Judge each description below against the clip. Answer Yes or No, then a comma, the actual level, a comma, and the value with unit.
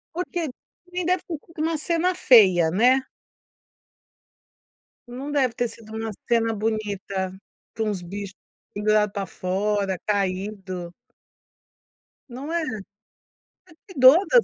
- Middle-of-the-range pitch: No, high, 220 Hz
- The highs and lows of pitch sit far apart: Yes, wide, 5.7 semitones